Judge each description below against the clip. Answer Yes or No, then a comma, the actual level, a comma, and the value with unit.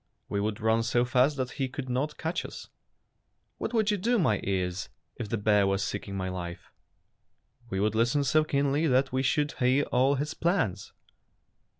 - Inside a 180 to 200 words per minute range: Yes, average, 190 wpm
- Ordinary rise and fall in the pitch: No, wide, 5.8 semitones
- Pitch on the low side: Yes, low, 125 Hz